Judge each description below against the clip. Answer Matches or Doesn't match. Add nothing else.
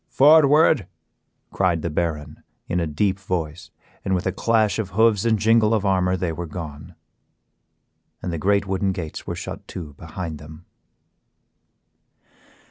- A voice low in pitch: Matches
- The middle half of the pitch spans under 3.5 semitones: Doesn't match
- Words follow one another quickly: Doesn't match